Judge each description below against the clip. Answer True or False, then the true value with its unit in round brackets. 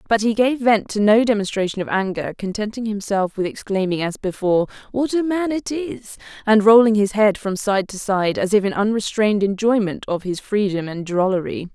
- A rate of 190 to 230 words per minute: True (195 wpm)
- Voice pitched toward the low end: False (210 Hz)